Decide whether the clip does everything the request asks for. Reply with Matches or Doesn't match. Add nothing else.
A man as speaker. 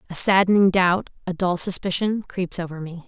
Doesn't match